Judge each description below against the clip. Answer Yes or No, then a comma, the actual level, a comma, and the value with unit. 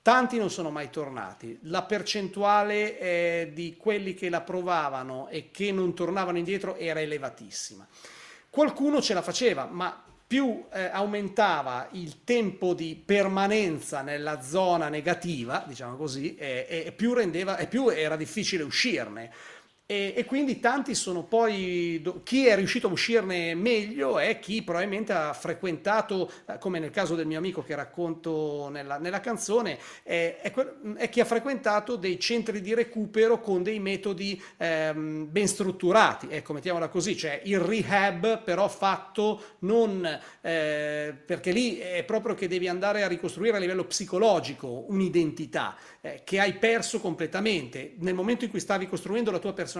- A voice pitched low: No, medium, 185 Hz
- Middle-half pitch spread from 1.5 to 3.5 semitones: No, average, 4.2 semitones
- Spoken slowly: No, average, 150 wpm